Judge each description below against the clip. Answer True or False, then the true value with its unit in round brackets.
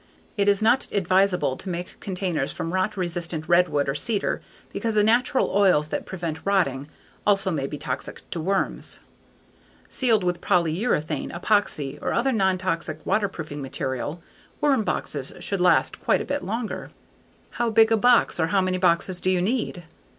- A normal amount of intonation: True (4.1 semitones)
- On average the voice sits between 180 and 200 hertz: True (185 Hz)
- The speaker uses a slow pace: False (165 wpm)